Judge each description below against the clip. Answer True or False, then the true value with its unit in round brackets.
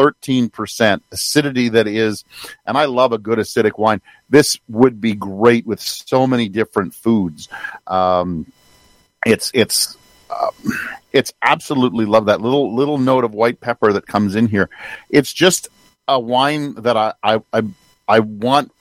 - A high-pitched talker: False (115 Hz)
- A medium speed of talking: True (155 wpm)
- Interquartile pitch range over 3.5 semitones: False (3.2 semitones)